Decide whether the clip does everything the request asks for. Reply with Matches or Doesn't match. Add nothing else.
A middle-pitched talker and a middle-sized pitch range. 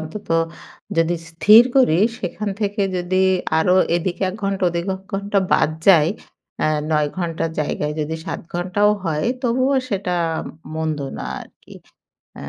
Matches